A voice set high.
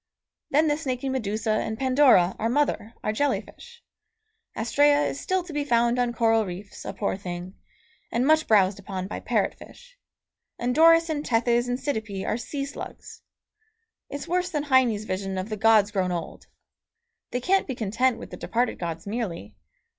Yes: high, 235 Hz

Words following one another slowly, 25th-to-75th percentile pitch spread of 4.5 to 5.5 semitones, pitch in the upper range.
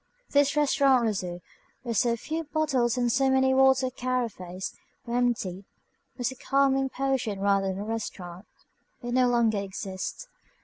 No: average, 145 wpm; average, 4.8 semitones; high, 245 Hz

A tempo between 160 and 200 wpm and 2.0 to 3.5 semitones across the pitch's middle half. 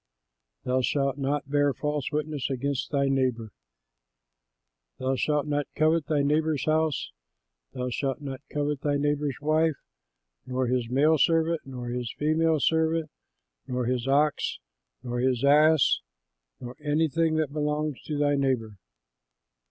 No: slow, 135 wpm; average, 2.8 semitones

